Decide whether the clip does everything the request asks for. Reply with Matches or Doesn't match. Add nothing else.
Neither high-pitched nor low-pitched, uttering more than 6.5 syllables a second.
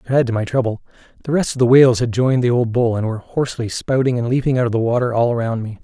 Doesn't match